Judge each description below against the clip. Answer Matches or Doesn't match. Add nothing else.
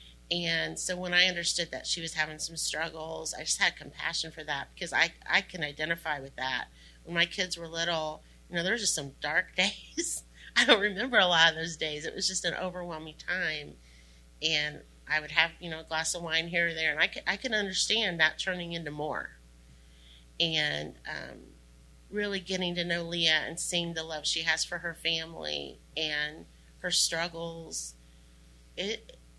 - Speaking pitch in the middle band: Matches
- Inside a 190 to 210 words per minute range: Matches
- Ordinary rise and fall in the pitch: Matches